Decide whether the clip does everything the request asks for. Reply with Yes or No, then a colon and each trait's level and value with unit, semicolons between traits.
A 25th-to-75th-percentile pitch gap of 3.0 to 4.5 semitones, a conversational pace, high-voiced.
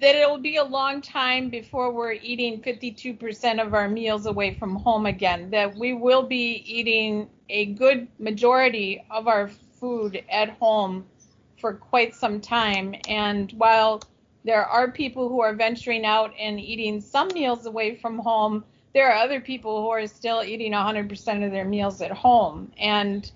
No: narrow, 2.6 semitones; average, 170 wpm; high, 225 Hz